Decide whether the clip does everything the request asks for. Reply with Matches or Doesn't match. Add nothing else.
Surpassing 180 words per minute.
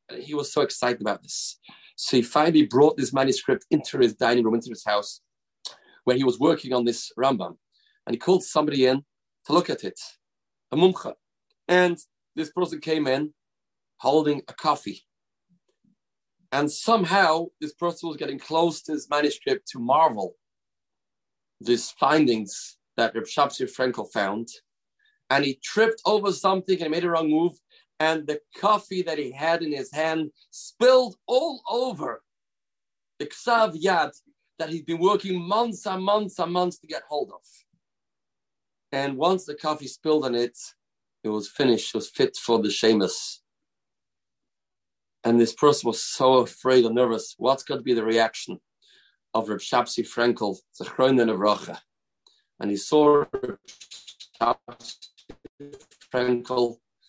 Doesn't match